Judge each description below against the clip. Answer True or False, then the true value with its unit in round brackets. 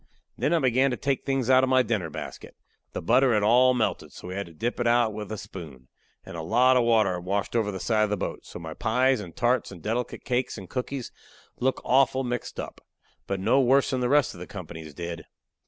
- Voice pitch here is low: True (115 Hz)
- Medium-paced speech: False (245 wpm)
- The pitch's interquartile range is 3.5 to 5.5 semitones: True (4.9 semitones)